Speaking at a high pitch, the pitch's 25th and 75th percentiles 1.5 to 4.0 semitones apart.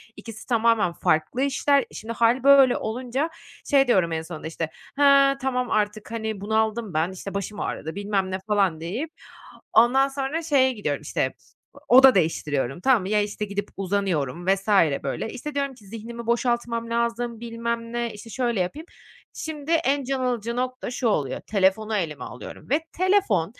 No: high, 230 Hz; average, 4.7 semitones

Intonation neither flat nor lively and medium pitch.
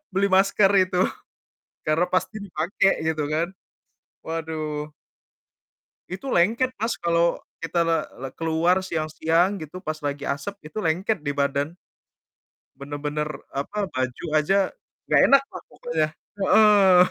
Yes: average, 3.8 semitones; medium, 165 Hz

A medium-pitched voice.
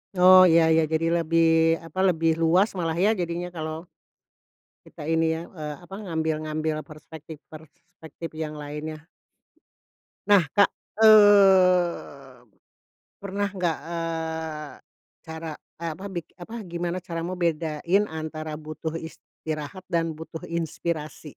Yes: medium, 165 Hz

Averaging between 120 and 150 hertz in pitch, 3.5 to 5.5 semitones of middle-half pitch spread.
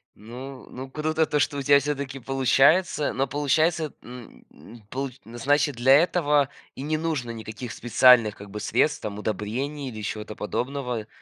Yes: low, 135 Hz; average, 3.8 semitones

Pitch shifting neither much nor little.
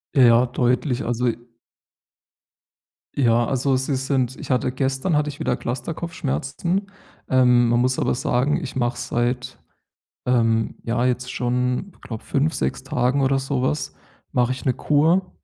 No: narrow, 2.2 semitones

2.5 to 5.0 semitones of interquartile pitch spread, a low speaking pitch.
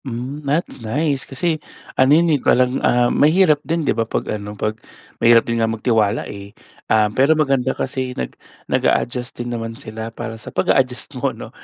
Yes: average, 3.7 semitones; low, 125 Hz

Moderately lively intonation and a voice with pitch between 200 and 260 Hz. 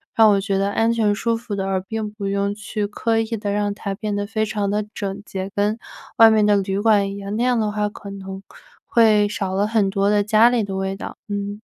No: narrow, 1.5 semitones; high, 205 Hz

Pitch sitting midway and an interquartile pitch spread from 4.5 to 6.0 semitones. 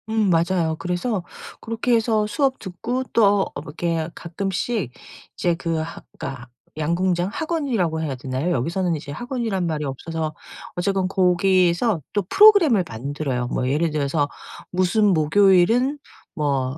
Yes: medium, 175 Hz; average, 5.2 semitones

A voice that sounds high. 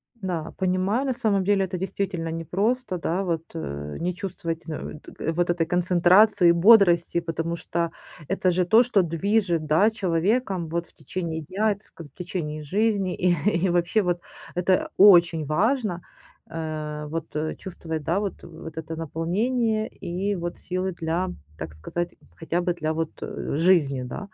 No: medium, 175 Hz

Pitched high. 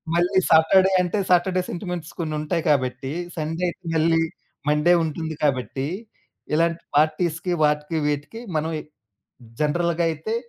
No: medium, 160 Hz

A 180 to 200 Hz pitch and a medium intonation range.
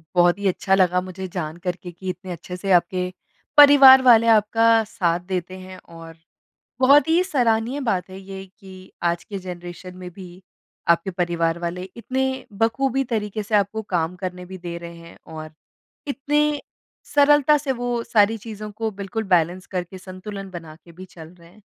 Yes: high, 190 Hz; average, 4.3 semitones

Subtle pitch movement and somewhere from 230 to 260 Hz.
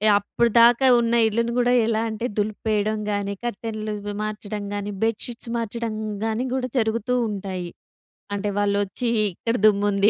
No: narrow, 2.3 semitones; high, 215 Hz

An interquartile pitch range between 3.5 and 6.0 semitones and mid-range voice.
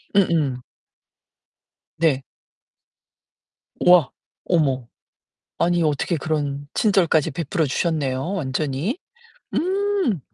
Yes: average, 4.5 semitones; medium, 160 Hz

